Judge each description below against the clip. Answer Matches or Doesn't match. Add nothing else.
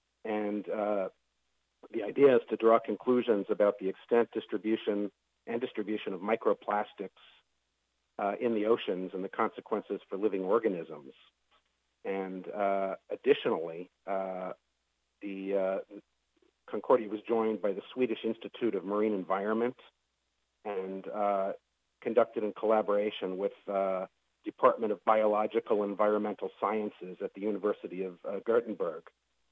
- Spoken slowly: Matches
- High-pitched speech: Doesn't match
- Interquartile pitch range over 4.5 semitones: Doesn't match